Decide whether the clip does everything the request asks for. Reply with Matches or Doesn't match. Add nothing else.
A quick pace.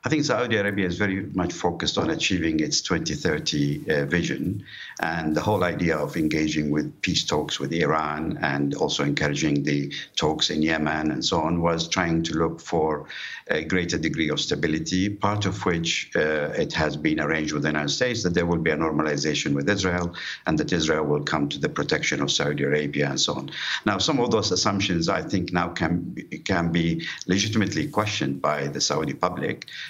Doesn't match